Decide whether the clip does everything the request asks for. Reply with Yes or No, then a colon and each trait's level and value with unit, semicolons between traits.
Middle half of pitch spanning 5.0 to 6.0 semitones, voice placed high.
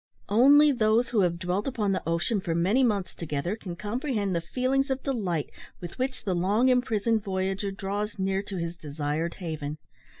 Yes: average, 5.3 semitones; high, 200 Hz